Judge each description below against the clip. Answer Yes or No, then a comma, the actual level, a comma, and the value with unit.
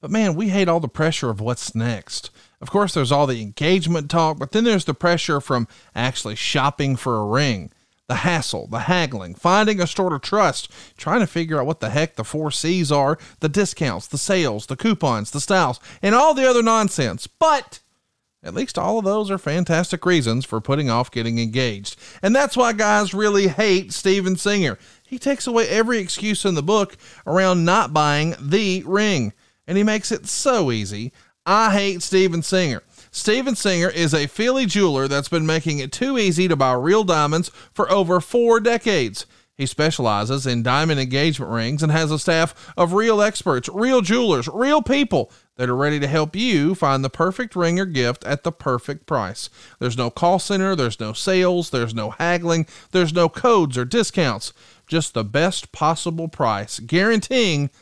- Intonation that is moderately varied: No, wide, 6.7 semitones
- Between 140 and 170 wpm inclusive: No, average, 185 wpm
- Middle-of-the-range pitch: Yes, medium, 165 Hz